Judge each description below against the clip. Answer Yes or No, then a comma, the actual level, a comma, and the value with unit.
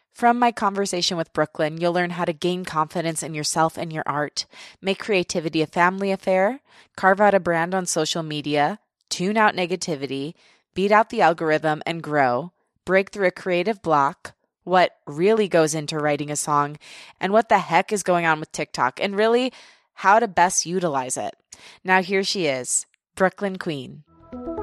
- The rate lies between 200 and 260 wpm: No, average, 175 wpm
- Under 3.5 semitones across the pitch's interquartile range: No, average, 3.8 semitones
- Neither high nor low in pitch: Yes, medium, 175 Hz